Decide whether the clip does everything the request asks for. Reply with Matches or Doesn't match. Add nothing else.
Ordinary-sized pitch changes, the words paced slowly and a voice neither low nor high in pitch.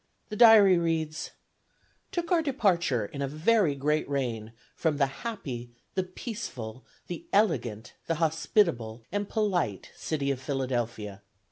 Doesn't match